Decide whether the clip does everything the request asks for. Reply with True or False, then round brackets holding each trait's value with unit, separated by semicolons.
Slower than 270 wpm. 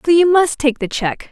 False (275 wpm)